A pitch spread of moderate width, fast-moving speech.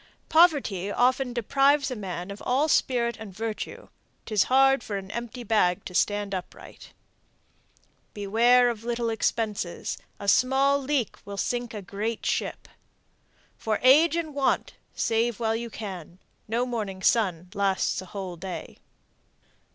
No: average, 4.0 semitones; average, 140 wpm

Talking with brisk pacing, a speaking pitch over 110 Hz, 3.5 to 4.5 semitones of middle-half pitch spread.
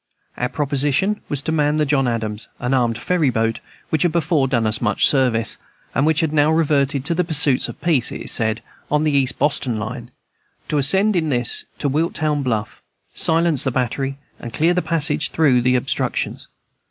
No: average, 190 wpm; medium, 140 Hz; average, 4.1 semitones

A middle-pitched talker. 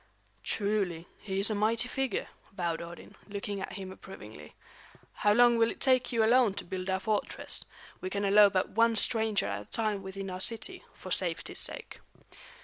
No: high, 200 Hz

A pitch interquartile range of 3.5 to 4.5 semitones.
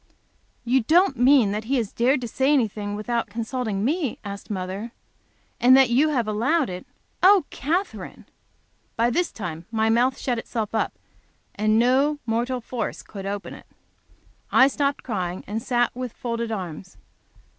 Yes: average, 3.8 semitones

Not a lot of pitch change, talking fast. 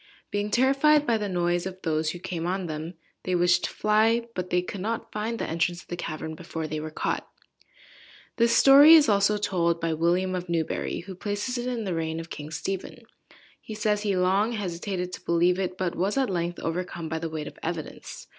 No: average, 3.8 semitones; fast, 210 wpm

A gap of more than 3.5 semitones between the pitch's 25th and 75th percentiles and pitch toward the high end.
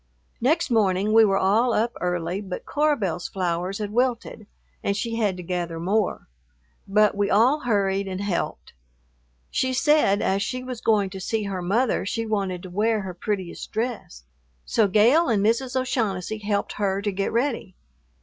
No: average, 3.2 semitones; high, 205 Hz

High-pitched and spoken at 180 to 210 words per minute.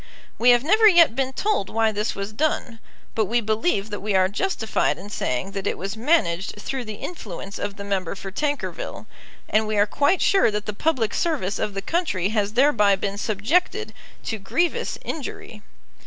Yes: high, 215 Hz; average, 185 wpm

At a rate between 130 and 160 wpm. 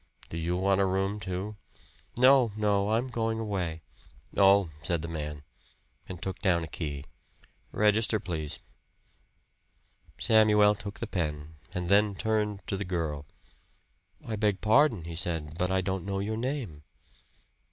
Yes: average, 145 wpm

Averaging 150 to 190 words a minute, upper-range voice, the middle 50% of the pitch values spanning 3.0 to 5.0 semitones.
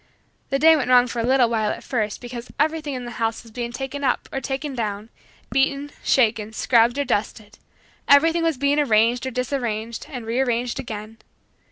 Yes: average, 185 wpm; high, 245 Hz; average, 3.3 semitones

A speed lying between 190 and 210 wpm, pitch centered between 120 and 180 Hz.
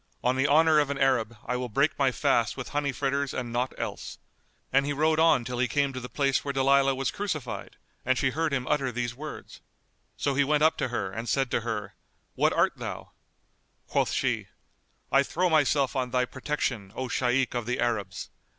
Yes: fast, 205 wpm; low, 135 Hz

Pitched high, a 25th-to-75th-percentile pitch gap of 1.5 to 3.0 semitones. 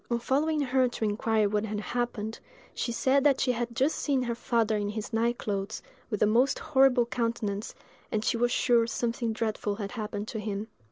Yes: high, 230 Hz; average, 2.7 semitones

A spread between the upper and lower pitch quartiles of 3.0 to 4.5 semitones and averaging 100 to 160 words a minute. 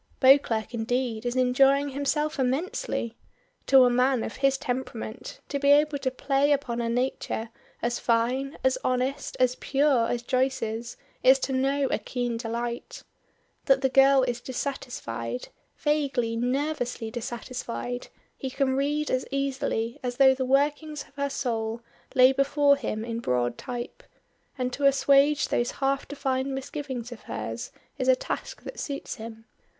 No: narrow, 2.6 semitones; average, 150 wpm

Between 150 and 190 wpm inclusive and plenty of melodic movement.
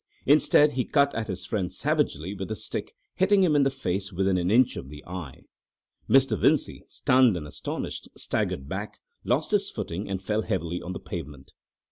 Yes: average, 185 wpm; wide, 6.7 semitones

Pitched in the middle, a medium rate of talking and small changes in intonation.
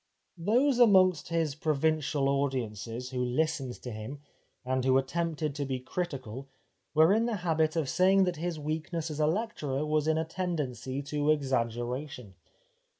No: medium, 150 Hz; average, 150 wpm; average, 4.1 semitones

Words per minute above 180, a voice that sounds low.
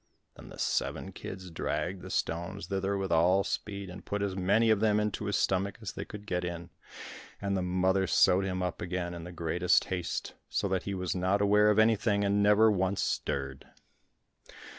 Yes: average, 195 wpm; very low, 95 Hz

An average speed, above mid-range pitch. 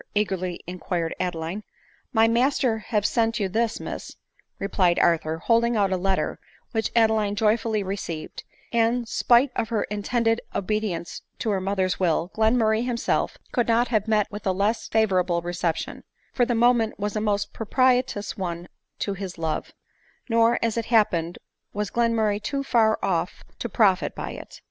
Yes: average, 165 wpm; high, 215 Hz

